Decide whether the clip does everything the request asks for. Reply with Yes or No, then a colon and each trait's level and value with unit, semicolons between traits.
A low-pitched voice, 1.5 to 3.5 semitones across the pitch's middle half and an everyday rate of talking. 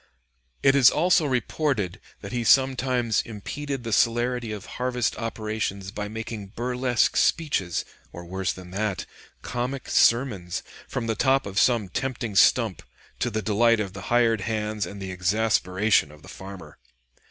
No: low, 110 Hz; average, 3.9 semitones; average, 150 wpm